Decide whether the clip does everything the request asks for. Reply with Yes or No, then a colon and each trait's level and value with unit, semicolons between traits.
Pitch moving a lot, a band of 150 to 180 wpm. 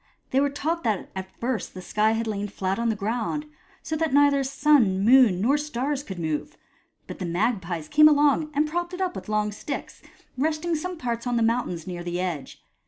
No: wide, 7.2 semitones; fast, 205 wpm